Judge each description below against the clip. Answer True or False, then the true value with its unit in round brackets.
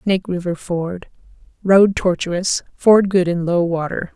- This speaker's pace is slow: True (130 wpm)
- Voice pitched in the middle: True (180 Hz)